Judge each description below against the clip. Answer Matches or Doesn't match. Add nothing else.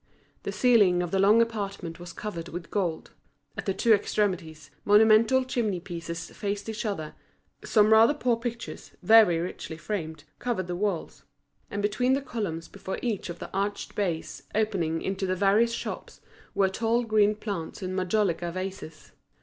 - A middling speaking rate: Matches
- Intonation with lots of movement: Doesn't match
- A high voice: Matches